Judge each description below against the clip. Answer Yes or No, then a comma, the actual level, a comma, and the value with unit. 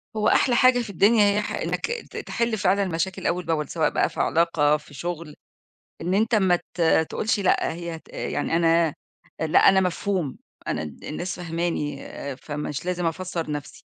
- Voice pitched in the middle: Yes, medium, 170 Hz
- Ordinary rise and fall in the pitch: Yes, average, 3.5 semitones